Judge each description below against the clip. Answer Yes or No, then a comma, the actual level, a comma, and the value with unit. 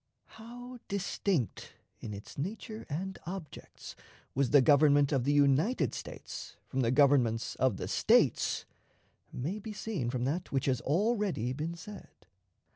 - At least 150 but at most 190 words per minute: No, average, 140 wpm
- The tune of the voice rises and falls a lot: Yes, wide, 7.3 semitones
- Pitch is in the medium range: Yes, medium, 145 Hz